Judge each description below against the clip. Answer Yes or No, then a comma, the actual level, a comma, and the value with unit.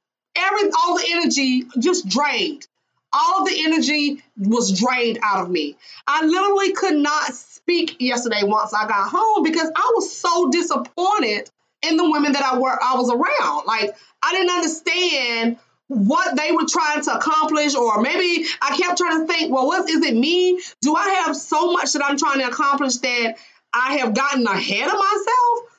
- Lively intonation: Yes, wide, 5.8 semitones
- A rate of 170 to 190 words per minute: Yes, average, 180 wpm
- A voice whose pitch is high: Yes, very high, 310 Hz